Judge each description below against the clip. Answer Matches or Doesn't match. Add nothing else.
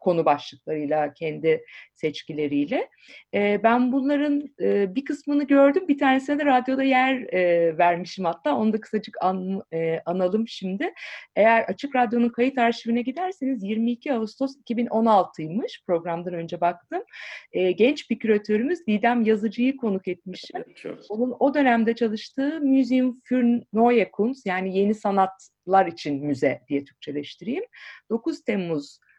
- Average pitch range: Doesn't match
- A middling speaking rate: Matches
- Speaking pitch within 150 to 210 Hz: Doesn't match